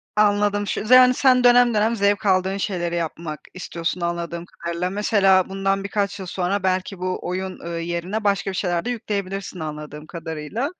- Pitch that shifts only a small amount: No, average, 3.1 semitones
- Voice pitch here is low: No, high, 190 Hz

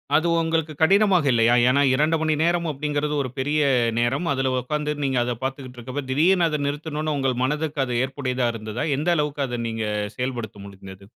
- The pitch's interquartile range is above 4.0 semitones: No, average, 3.5 semitones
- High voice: No, medium, 140 Hz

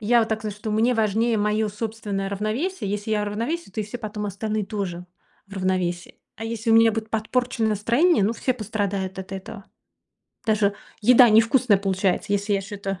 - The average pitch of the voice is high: Yes, high, 215 Hz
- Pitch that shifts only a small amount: Yes, narrow, 2.2 semitones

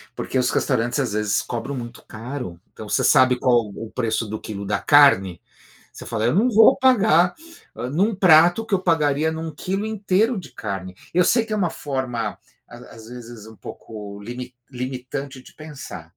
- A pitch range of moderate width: No, wide, 7.1 semitones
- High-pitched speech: No, low, 130 Hz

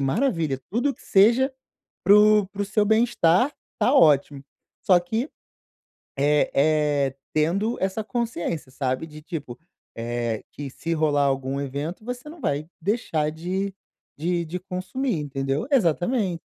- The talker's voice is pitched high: No, medium, 170 Hz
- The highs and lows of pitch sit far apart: Yes, wide, 6.6 semitones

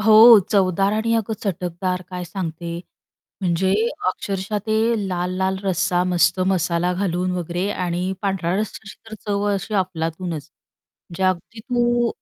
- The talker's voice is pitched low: No, medium, 185 Hz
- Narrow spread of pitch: Yes, narrow, 2.3 semitones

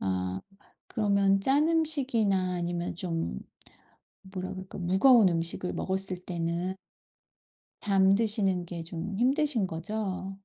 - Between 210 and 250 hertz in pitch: No, high, 190 Hz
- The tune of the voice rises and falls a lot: No, average, 3.3 semitones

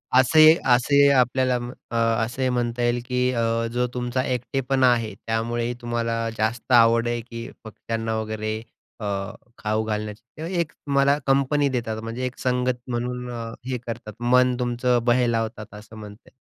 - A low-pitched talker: Yes, low, 120 Hz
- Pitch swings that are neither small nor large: No, narrow, 1.9 semitones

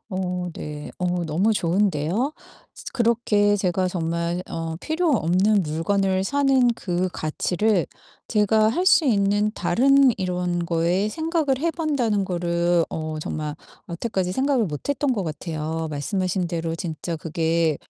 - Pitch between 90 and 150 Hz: No, medium, 185 Hz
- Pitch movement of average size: Yes, average, 4.8 semitones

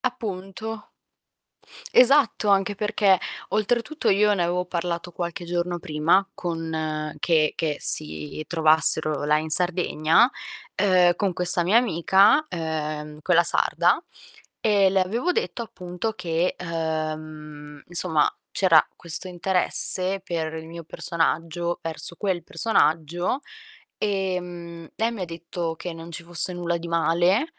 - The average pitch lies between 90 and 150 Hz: No, medium, 175 Hz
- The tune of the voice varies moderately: Yes, average, 3.1 semitones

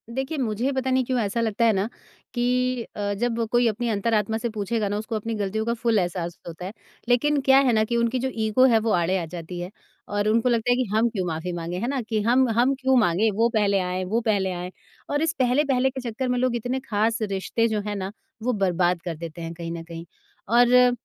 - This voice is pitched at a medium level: No, high, 220 Hz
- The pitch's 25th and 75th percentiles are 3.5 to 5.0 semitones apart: Yes, average, 4.3 semitones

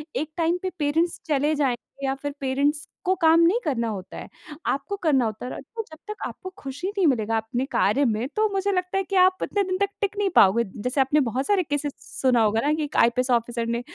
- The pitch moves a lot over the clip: Yes, wide, 6.5 semitones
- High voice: Yes, very high, 290 Hz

